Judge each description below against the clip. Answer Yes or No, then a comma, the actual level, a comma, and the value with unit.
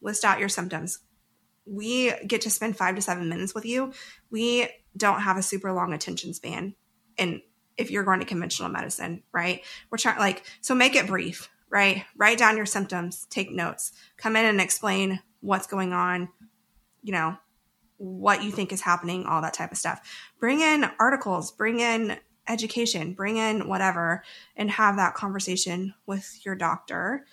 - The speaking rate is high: No, average, 175 wpm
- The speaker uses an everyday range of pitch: Yes, average, 3.3 semitones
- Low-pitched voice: No, high, 200 Hz